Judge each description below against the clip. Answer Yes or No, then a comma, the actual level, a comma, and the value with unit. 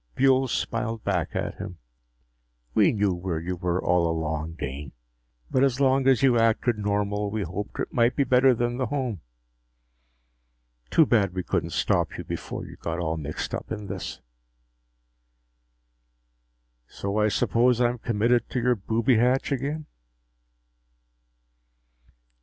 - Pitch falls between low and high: No, low, 110 Hz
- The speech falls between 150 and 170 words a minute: No, average, 140 wpm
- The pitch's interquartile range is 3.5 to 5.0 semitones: No, wide, 5.4 semitones